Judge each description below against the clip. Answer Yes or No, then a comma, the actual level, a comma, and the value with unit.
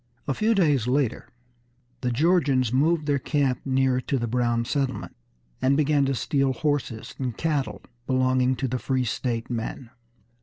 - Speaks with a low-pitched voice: Yes, low, 130 Hz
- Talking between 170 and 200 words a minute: No, average, 155 wpm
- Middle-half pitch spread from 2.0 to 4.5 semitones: Yes, narrow, 2.6 semitones